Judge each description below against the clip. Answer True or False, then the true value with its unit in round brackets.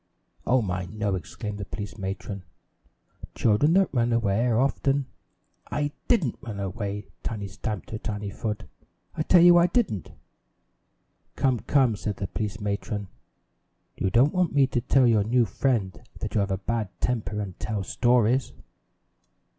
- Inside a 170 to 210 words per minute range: False (160 wpm)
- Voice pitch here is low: True (110 Hz)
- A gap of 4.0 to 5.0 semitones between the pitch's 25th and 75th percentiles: True (4.3 semitones)